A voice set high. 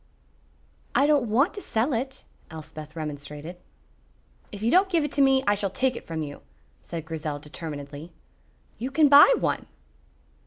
Yes: high, 205 Hz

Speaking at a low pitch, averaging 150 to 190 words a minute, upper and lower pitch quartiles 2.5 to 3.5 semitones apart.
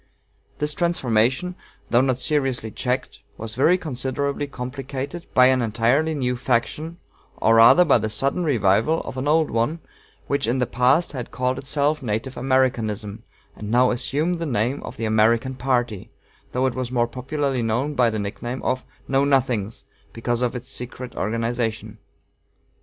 Yes: low, 125 Hz; average, 160 wpm; average, 3.1 semitones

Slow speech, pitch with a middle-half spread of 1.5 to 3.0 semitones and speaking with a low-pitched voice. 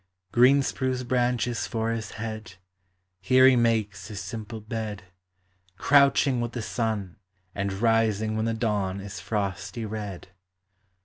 Yes: slow, 130 wpm; average, 2.7 semitones; low, 110 Hz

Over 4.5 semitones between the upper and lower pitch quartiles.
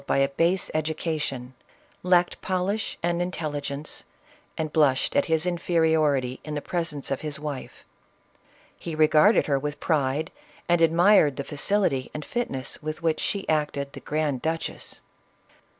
No: average, 3.1 semitones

